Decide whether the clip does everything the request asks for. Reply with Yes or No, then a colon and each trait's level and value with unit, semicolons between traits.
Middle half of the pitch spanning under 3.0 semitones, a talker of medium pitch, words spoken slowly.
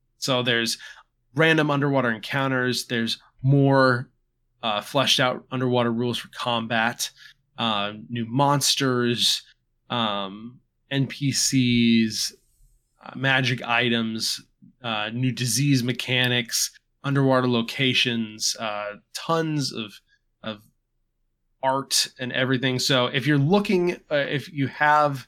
No: narrow, 2.6 semitones; low, 125 Hz; slow, 100 wpm